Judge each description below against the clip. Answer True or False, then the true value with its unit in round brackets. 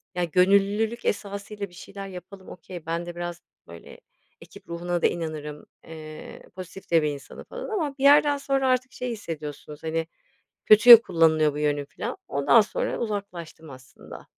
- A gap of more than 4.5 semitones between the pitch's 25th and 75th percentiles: True (5.0 semitones)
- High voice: False (175 Hz)